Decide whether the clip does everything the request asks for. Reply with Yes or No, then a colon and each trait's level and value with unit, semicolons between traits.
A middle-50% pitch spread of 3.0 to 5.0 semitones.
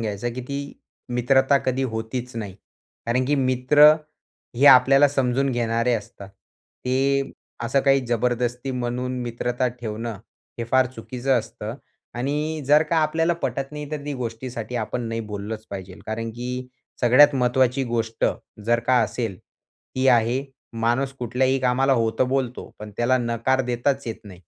No: narrow, 2.5 semitones